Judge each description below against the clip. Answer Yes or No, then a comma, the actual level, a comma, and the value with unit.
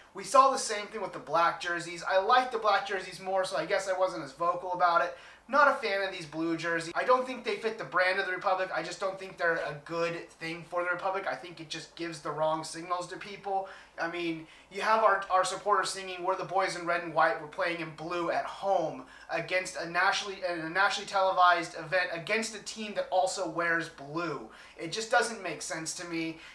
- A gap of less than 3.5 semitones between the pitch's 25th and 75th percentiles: Yes, narrow, 2.6 semitones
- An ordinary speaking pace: No, fast, 235 wpm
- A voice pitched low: No, medium, 180 Hz